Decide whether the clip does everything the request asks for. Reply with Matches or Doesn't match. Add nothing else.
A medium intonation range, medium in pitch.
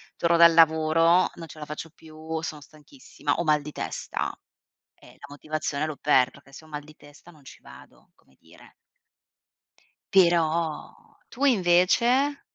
Doesn't match